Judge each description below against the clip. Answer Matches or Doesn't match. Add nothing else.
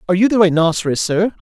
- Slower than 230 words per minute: Matches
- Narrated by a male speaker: Matches